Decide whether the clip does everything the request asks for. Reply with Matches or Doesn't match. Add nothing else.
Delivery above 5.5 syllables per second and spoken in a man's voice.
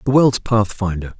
Doesn't match